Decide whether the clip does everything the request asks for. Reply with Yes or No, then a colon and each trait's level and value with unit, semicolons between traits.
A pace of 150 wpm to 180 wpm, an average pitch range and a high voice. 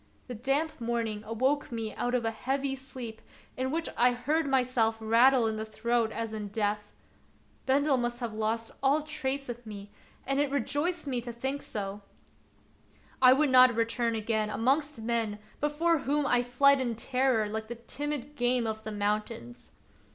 Yes: average, 175 wpm; average, 3.6 semitones; high, 240 Hz